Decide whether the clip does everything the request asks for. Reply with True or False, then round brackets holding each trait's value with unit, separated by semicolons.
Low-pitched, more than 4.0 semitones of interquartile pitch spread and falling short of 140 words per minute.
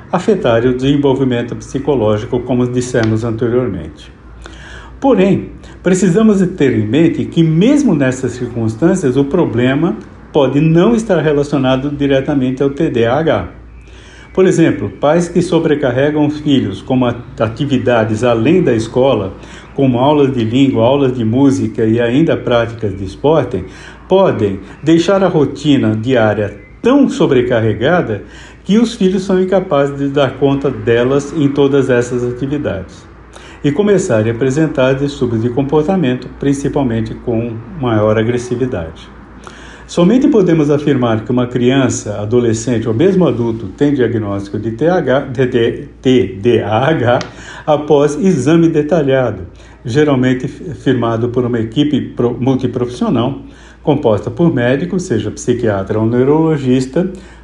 True (130 Hz; 4.4 semitones; 120 wpm)